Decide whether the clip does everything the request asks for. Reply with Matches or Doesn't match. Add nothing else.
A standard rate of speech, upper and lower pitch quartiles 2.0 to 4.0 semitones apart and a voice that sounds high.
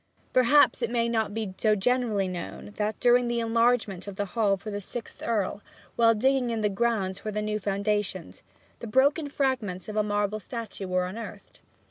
Matches